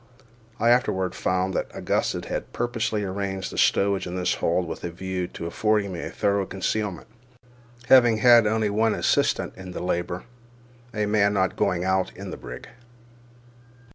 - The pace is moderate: Yes, average, 165 wpm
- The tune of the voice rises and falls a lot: No, average, 2.7 semitones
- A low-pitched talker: Yes, low, 100 Hz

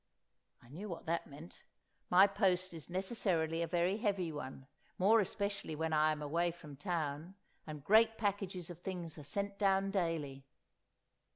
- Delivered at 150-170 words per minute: Yes, average, 160 wpm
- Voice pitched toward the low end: No, medium, 175 Hz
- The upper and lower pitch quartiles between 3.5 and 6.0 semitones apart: Yes, average, 3.9 semitones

